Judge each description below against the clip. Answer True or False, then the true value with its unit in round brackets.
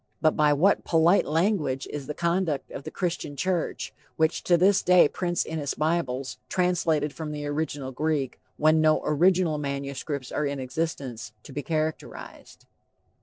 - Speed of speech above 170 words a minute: False (160 wpm)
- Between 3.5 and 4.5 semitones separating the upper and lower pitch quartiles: False (3.1 semitones)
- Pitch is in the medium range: True (155 Hz)